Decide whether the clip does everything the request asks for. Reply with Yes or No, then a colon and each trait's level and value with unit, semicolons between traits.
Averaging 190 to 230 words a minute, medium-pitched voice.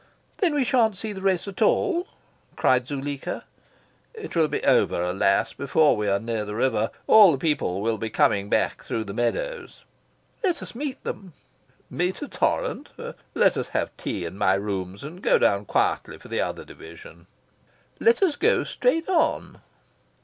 No: average, 170 wpm; medium, 145 Hz